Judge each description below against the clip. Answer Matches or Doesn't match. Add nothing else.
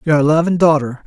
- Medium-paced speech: Matches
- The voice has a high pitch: Doesn't match